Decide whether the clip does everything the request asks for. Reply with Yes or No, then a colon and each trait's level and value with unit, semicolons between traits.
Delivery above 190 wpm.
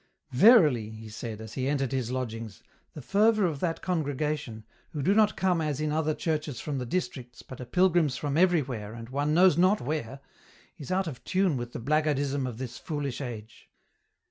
Yes: average, 200 wpm